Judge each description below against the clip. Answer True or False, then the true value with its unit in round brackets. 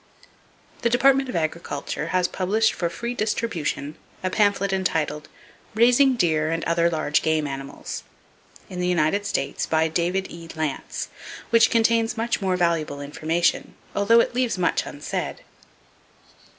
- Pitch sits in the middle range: True (180 Hz)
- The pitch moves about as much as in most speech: False (6.0 semitones)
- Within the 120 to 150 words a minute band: True (135 wpm)